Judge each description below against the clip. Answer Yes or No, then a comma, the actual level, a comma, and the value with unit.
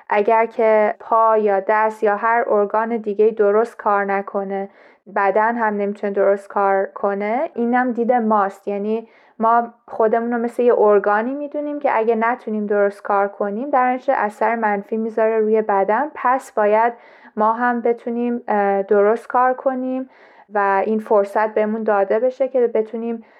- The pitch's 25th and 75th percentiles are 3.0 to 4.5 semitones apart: No, narrow, 2.4 semitones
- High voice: Yes, high, 220 Hz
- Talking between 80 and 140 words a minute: No, average, 150 wpm